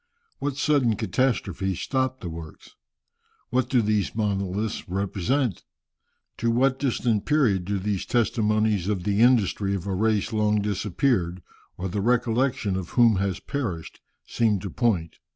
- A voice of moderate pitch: No, low, 105 Hz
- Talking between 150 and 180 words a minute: No, average, 140 wpm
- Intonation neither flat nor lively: Yes, average, 4.1 semitones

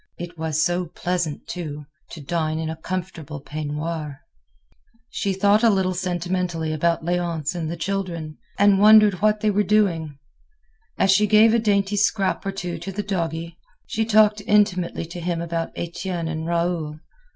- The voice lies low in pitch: No, medium, 175 Hz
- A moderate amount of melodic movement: Yes, average, 3.4 semitones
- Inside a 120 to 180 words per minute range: Yes, average, 160 wpm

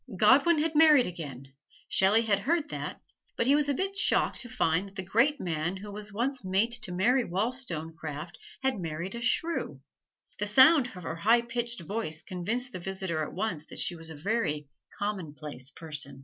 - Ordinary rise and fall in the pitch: No, wide, 7.1 semitones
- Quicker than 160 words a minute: Yes, average, 185 wpm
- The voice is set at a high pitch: Yes, high, 200 Hz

